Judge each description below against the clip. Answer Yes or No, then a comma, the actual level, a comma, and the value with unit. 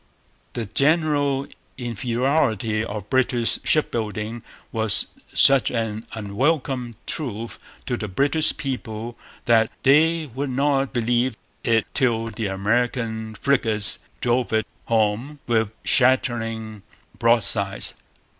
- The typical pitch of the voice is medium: No, low, 120 Hz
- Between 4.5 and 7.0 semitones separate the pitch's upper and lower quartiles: No, average, 3.3 semitones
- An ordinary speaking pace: No, slow, 100 wpm